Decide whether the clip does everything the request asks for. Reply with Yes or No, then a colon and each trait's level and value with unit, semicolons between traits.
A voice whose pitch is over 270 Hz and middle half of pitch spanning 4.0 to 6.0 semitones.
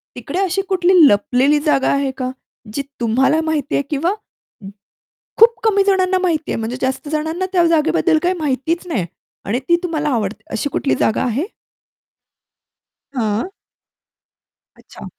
Yes: very high, 300 Hz; average, 5.3 semitones